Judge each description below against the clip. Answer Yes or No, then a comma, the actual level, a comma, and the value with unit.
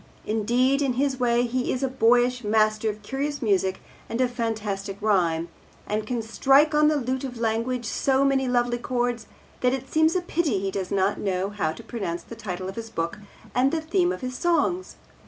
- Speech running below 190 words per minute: No, average, 200 wpm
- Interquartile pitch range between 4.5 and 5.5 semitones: No, average, 4.1 semitones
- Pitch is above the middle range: Yes, high, 240 Hz